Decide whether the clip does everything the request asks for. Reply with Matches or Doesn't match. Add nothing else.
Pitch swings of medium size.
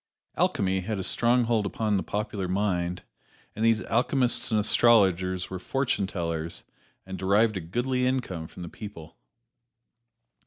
Matches